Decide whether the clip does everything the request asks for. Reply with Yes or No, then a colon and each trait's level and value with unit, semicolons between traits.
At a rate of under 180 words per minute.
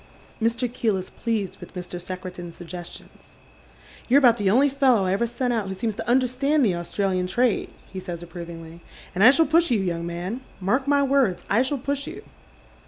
No: average, 200 wpm